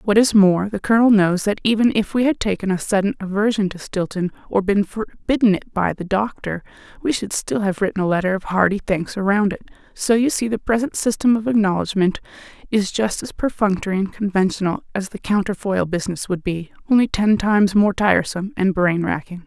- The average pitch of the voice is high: Yes, high, 200 Hz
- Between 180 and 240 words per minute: Yes, average, 195 wpm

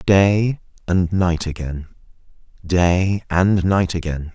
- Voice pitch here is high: No, very low, 90 Hz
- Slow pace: Yes, slow, 110 wpm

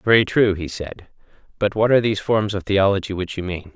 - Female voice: No, male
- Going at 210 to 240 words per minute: Yes, fast, 225 wpm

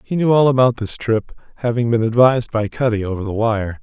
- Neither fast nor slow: No, fast, 220 wpm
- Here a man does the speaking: Yes, male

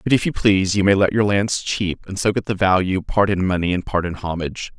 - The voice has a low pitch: Yes, very low, 95 Hz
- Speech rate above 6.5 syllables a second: No, 5.7 syllables/s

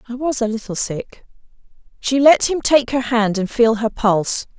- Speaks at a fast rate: No, average, 195 wpm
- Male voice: No, female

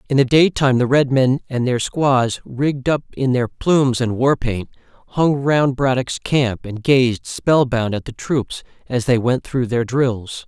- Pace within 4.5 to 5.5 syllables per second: No, 4.1 syllables/s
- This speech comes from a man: Yes, male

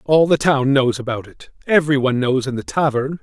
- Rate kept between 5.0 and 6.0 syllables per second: Yes, 5.7 syllables/s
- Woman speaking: No, male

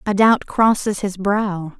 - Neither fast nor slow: Yes, average, 165 wpm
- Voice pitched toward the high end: Yes, high, 200 Hz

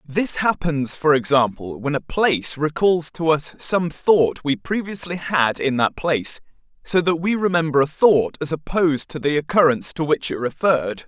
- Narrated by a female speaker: No, male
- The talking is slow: No, average, 180 wpm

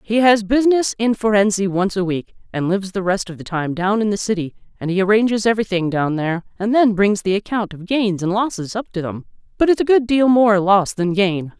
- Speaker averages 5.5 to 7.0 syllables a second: Yes, 5.7 syllables/s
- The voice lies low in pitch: No, high, 200 Hz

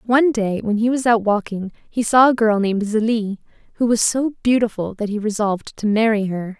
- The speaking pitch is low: No, high, 220 Hz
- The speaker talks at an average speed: No, fast, 210 wpm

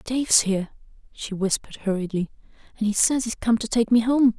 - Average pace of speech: Yes, average, 190 wpm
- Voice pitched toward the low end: No, high, 220 Hz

